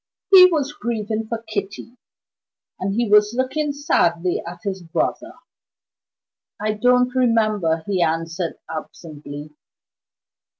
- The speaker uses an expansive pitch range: Yes, wide, 6.5 semitones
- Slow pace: Yes, slow, 110 wpm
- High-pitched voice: Yes, high, 210 Hz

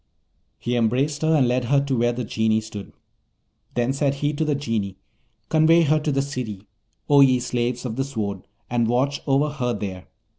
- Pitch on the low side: Yes, low, 125 Hz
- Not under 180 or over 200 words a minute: Yes, average, 190 wpm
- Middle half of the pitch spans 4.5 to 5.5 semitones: No, average, 3.8 semitones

